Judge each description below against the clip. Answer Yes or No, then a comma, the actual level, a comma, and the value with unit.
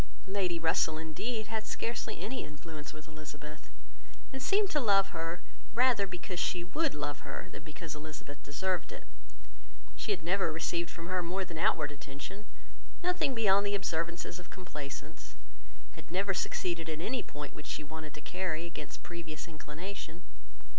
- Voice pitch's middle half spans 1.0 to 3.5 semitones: No, average, 4.1 semitones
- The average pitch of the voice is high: No, medium, 170 Hz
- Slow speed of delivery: No, average, 160 wpm